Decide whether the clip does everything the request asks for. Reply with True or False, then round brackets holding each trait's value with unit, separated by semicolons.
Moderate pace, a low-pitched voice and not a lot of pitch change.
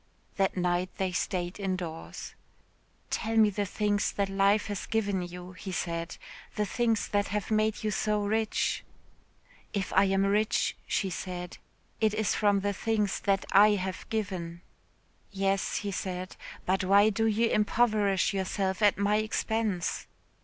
False (150 wpm; 200 Hz; 2.2 semitones)